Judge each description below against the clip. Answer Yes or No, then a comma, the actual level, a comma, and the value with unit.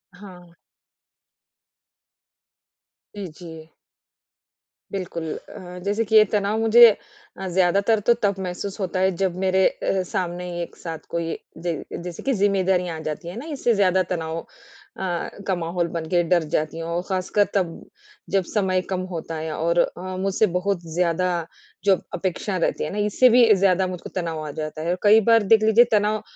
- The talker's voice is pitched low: No, medium, 185 Hz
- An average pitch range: Yes, average, 3.0 semitones